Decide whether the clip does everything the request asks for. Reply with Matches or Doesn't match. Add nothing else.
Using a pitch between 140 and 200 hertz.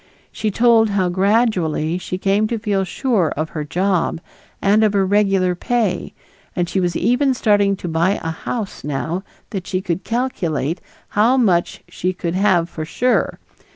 Matches